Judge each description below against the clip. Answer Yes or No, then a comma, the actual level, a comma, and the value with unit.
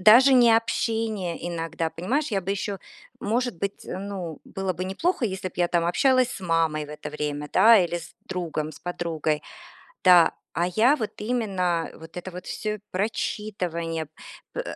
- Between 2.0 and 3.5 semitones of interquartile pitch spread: No, average, 4.5 semitones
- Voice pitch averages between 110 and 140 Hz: No, medium, 185 Hz